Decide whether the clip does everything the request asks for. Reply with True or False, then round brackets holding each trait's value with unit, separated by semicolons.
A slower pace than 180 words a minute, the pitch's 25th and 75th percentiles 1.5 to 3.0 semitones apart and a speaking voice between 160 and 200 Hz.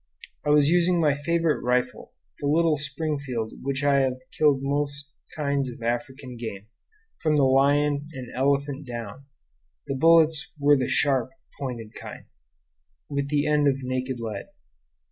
False (150 wpm; 2.4 semitones; 140 Hz)